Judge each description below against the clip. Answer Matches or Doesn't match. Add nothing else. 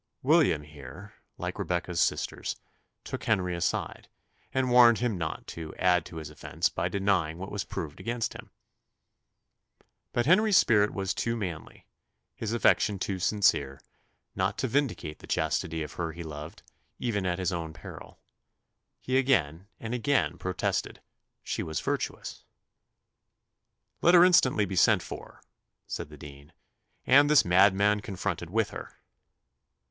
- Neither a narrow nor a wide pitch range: Doesn't match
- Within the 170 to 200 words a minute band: Doesn't match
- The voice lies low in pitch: Matches